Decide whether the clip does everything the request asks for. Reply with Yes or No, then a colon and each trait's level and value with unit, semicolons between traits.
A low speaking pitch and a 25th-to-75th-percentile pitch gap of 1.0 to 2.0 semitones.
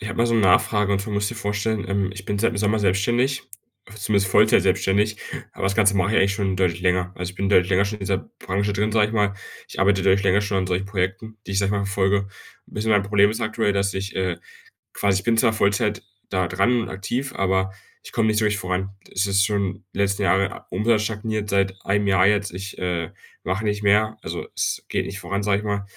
Yes: low, 100 Hz; narrow, 1.6 semitones